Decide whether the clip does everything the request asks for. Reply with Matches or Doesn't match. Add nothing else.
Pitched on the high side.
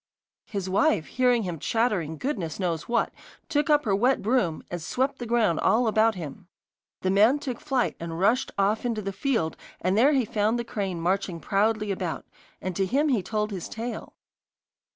Matches